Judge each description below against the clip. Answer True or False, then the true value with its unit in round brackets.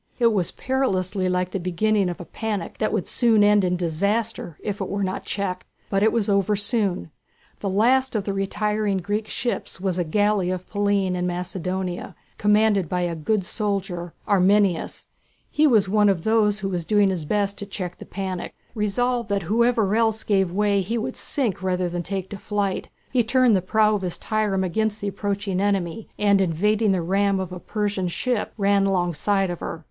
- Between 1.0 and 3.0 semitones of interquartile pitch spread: True (2.6 semitones)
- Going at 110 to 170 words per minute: False (195 wpm)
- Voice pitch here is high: True (200 Hz)